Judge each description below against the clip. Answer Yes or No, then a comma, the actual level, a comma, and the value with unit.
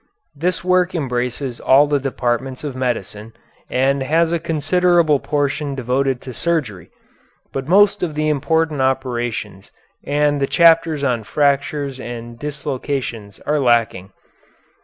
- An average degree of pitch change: Yes, average, 3.8 semitones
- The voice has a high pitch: No, medium, 140 Hz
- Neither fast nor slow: No, slow, 125 wpm